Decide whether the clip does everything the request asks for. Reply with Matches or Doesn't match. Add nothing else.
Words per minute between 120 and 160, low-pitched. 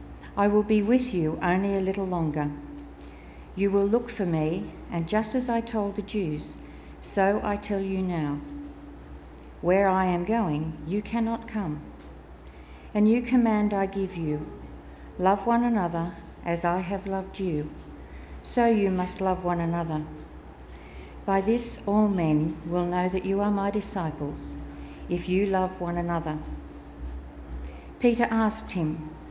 Doesn't match